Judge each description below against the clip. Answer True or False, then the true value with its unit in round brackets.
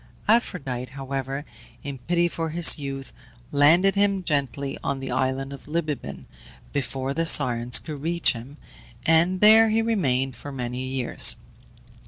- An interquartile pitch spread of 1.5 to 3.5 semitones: False (4.4 semitones)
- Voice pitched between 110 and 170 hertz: True (140 Hz)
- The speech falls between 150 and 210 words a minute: False (140 wpm)